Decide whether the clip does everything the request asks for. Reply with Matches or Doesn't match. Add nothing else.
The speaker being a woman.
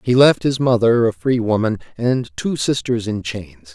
Doesn't match